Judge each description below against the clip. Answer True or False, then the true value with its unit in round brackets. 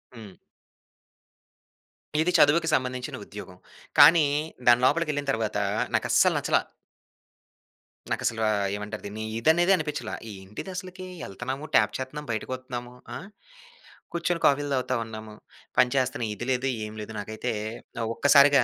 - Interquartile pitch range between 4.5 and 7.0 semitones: True (5.2 semitones)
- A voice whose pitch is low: True (130 Hz)